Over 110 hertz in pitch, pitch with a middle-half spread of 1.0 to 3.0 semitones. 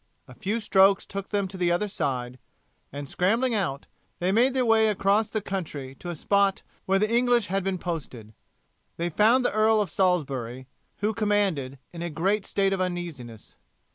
No: high, 190 Hz; average, 4.7 semitones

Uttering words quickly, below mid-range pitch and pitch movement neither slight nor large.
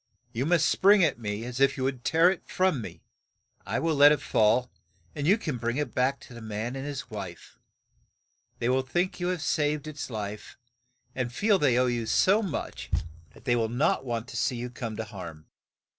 Yes: fast, 215 wpm; low, 130 Hz; average, 4.5 semitones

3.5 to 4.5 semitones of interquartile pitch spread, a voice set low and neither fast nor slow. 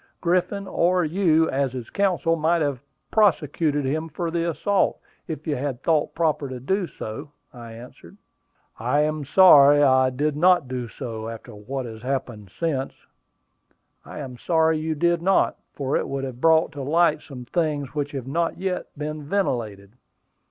No: average, 4.2 semitones; medium, 150 Hz; average, 165 wpm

